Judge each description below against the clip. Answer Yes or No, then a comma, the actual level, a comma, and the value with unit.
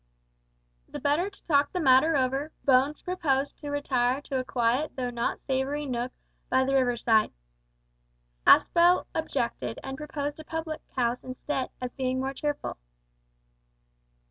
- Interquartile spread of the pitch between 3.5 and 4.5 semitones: No, narrow, 2.6 semitones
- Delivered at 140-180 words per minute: Yes, average, 145 wpm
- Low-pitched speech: No, very high, 270 Hz